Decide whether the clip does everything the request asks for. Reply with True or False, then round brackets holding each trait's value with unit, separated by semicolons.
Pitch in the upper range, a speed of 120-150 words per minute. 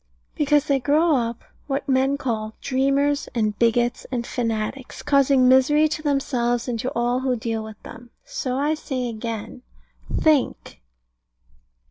True (260 Hz; 140 wpm)